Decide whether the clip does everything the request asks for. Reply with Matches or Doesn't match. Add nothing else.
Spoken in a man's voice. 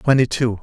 Matches